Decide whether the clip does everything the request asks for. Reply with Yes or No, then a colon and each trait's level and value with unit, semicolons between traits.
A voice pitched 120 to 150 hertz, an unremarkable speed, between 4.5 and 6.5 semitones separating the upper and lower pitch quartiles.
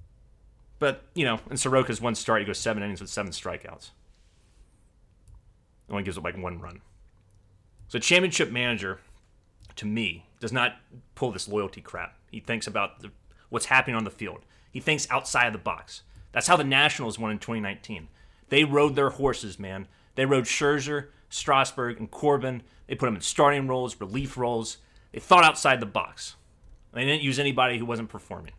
No: low, 110 Hz; average, 175 wpm; average, 4.8 semitones